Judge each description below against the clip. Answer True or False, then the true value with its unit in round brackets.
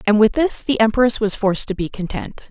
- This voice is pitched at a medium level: False (215 Hz)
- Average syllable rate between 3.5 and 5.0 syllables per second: False (5.5 syllables/s)